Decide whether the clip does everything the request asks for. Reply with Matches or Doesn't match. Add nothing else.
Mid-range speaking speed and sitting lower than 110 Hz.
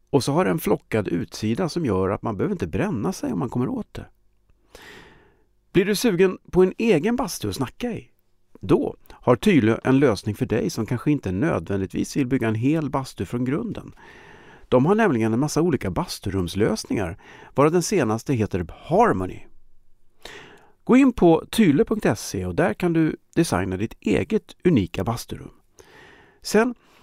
Doesn't match